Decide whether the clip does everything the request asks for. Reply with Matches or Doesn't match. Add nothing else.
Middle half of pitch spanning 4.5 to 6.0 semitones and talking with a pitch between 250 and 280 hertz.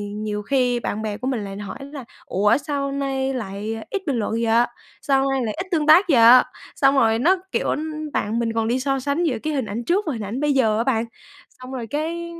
Doesn't match